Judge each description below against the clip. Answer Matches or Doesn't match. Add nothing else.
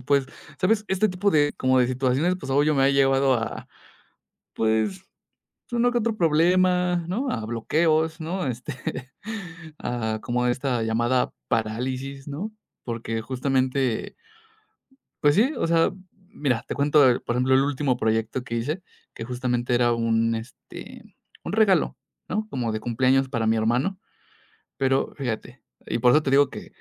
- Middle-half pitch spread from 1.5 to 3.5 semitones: Doesn't match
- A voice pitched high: Doesn't match